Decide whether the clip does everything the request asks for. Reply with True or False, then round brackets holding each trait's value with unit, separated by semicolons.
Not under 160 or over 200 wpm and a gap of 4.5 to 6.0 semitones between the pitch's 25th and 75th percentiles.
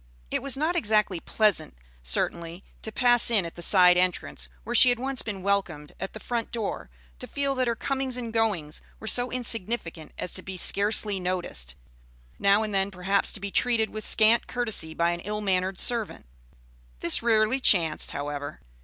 True (185 wpm; 4.8 semitones)